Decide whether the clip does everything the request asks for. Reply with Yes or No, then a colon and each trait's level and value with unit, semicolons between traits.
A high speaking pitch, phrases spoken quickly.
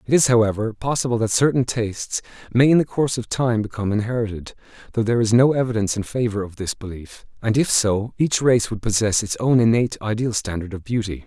No: low, 110 Hz; fast, 210 wpm